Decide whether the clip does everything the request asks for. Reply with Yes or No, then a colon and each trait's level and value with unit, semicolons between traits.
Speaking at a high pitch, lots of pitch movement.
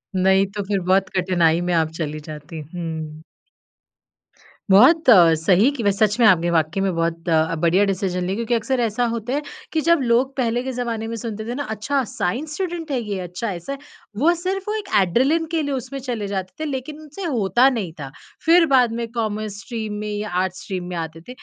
Yes: high, 215 Hz; wide, 6.4 semitones